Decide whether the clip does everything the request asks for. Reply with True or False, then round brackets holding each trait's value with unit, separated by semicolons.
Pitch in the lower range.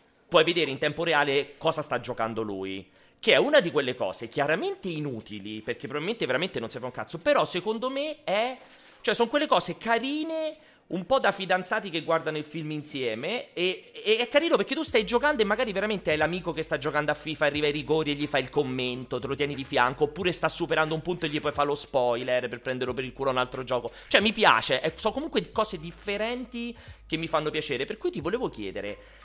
False (160 Hz)